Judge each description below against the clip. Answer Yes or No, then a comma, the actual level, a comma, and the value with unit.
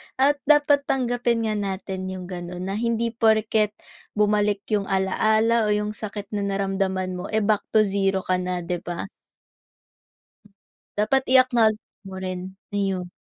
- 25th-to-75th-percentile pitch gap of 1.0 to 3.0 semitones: Yes, average, 2.7 semitones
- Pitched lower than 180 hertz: No, high, 205 Hz